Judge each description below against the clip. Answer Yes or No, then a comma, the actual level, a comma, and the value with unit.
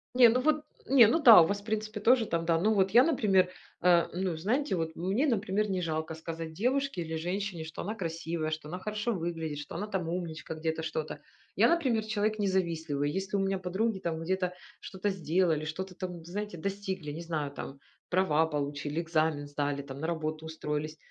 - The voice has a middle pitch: Yes, medium, 175 Hz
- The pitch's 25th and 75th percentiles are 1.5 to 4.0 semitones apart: No, average, 4.4 semitones